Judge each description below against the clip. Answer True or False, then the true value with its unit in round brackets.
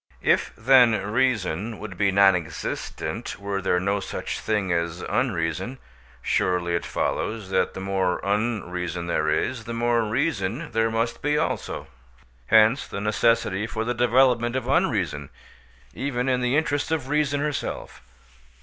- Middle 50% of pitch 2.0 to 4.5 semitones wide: False (4.9 semitones)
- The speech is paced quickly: False (145 wpm)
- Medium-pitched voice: False (110 Hz)